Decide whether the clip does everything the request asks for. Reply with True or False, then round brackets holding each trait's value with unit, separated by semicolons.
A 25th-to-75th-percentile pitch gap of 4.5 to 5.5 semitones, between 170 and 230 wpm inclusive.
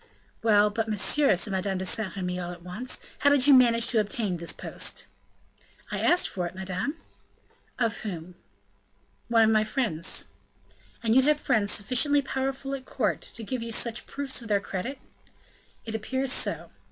True (5.2 semitones; 175 wpm)